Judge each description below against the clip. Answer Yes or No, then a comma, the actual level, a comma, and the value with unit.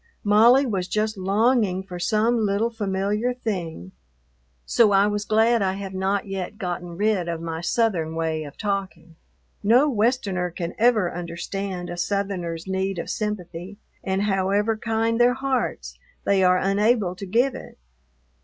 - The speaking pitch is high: Yes, high, 200 Hz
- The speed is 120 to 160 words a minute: Yes, average, 150 wpm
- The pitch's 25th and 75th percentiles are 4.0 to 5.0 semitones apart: No, average, 3.5 semitones